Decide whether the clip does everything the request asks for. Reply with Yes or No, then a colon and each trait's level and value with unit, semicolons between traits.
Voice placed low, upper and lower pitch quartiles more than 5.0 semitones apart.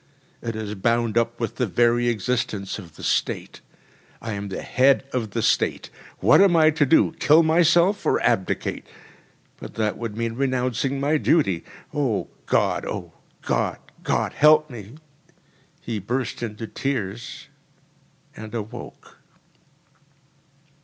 No: low, 120 Hz; average, 4.3 semitones